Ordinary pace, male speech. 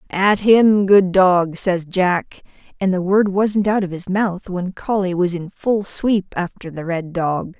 No: average, 190 wpm; female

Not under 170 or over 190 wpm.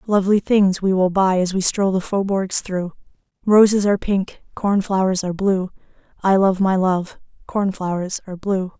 Yes: average, 175 wpm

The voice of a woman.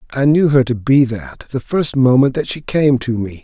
No: male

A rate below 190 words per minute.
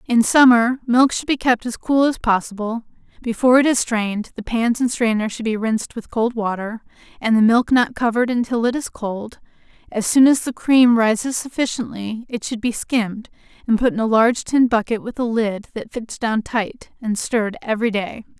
No: average, 200 wpm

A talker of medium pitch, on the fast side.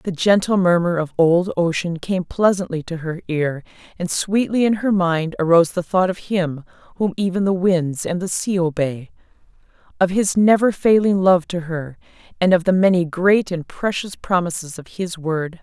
No: medium, 180 Hz; average, 180 wpm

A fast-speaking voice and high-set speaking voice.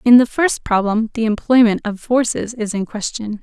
No: average, 195 wpm; high, 225 Hz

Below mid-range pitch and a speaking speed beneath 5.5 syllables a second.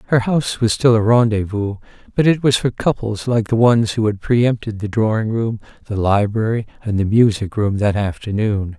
Yes: low, 110 Hz; 5.1 syllables/s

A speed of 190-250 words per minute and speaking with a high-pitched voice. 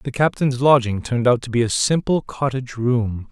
No: average, 200 wpm; low, 125 Hz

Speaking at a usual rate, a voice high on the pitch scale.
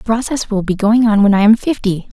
No: fast, 275 wpm; high, 215 Hz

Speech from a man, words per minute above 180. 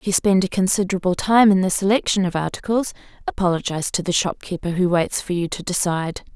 No: female; average, 200 wpm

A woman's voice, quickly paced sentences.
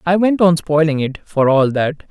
No: male; fast, 230 wpm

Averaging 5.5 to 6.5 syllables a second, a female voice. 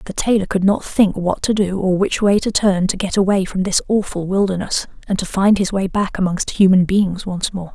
No: 5.2 syllables/s; female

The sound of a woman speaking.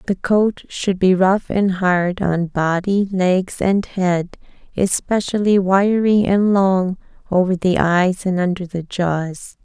Yes: female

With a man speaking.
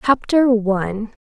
No: female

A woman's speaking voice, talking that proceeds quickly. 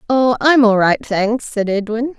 No: female; average, 190 wpm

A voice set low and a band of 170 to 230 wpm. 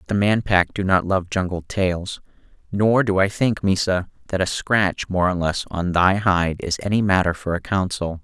Yes: very low, 95 Hz; fast, 205 wpm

